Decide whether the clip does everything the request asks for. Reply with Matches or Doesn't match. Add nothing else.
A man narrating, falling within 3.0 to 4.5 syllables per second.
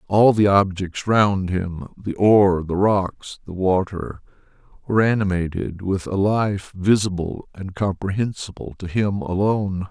Matches